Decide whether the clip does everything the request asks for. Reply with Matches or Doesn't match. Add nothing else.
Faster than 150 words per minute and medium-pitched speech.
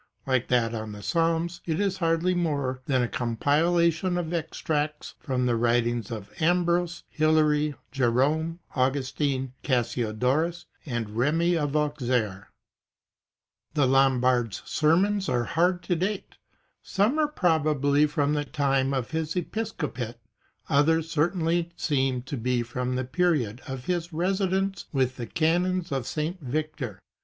Doesn't match